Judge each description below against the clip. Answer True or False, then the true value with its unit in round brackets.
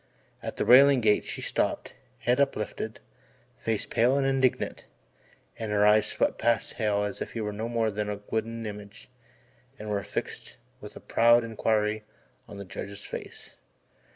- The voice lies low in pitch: True (110 Hz)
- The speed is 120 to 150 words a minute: False (160 wpm)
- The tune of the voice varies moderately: False (2.1 semitones)